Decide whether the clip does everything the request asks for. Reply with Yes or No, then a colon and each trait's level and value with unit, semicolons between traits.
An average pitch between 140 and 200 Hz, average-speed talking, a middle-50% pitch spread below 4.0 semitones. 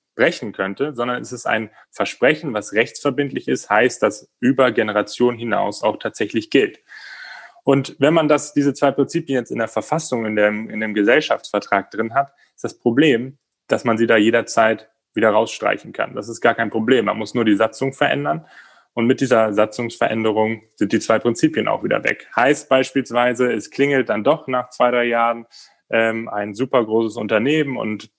No: low, 120 Hz; average, 180 wpm; average, 3.5 semitones